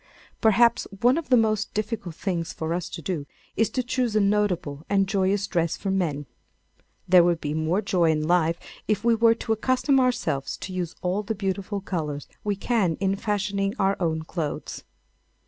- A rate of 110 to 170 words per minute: No, average, 180 wpm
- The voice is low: No, high, 195 Hz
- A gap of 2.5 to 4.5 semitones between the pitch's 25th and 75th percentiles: Yes, average, 4.2 semitones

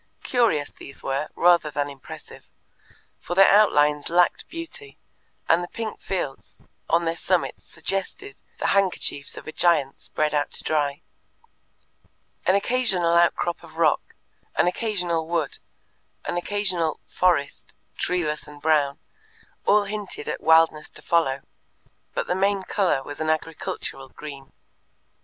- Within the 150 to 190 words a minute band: No, slow, 135 wpm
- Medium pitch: Yes, medium, 170 Hz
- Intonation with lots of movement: No, average, 4.2 semitones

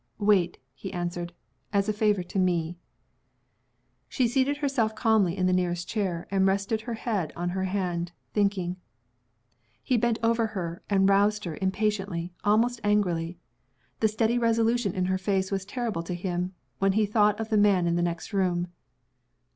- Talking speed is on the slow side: No, average, 165 wpm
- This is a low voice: No, high, 195 Hz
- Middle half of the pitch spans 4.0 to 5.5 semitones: No, average, 3.4 semitones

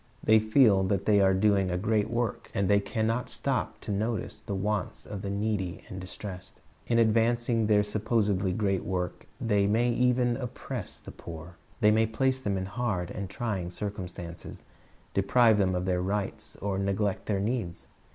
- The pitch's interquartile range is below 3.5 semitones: Yes, average, 2.8 semitones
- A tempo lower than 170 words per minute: No, average, 175 wpm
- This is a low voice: Yes, low, 105 Hz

